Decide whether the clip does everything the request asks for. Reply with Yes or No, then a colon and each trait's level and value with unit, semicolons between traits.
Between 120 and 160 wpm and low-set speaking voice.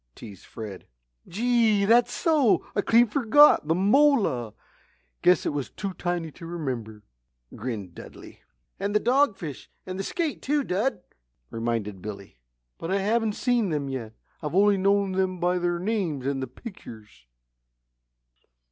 No: average, 145 wpm; medium, 185 Hz